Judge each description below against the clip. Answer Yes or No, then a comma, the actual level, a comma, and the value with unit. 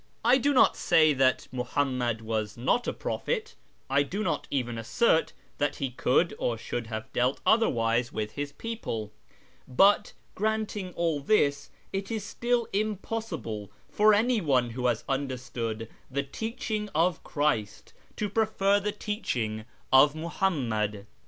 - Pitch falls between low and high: Yes, medium, 145 Hz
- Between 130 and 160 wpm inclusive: Yes, average, 140 wpm